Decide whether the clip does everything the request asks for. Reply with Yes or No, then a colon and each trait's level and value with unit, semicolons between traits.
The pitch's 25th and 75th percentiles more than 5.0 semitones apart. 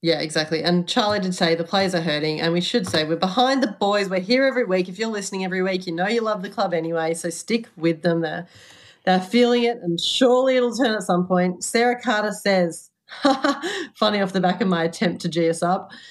Yes: wide, 5.5 semitones